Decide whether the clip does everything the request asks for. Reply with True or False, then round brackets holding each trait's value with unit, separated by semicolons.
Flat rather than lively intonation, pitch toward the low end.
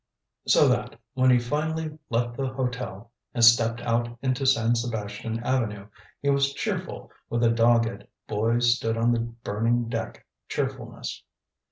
True (1.9 semitones; 120 Hz)